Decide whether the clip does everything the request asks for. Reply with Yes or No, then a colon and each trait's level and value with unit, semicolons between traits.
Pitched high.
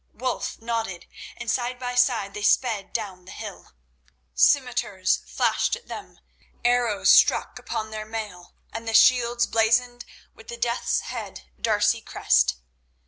Yes: high, 225 Hz